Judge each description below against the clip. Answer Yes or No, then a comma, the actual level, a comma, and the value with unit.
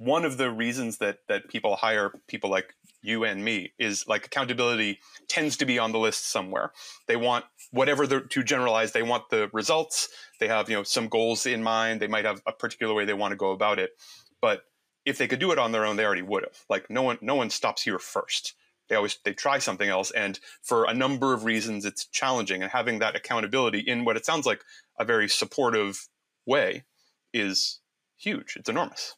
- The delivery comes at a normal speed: No, fast, 215 wpm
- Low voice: Yes, low, 115 Hz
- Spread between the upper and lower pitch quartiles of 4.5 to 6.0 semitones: No, average, 3.8 semitones